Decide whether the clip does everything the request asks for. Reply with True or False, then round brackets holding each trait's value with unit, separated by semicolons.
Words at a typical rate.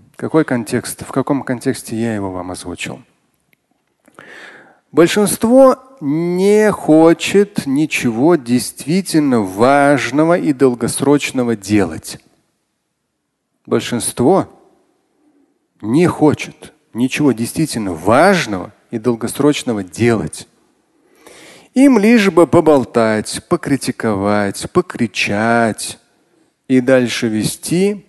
False (75 wpm)